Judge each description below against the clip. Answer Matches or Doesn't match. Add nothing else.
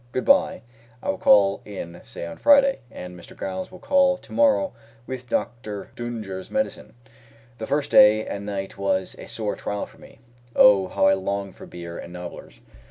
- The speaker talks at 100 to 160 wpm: Doesn't match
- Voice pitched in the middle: Doesn't match